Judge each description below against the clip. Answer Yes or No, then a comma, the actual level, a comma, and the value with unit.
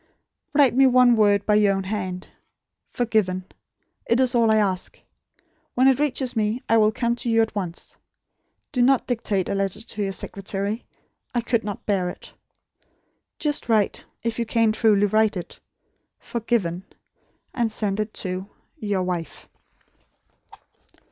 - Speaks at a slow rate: No, average, 150 wpm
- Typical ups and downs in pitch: Yes, average, 3.2 semitones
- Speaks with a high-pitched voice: Yes, high, 215 Hz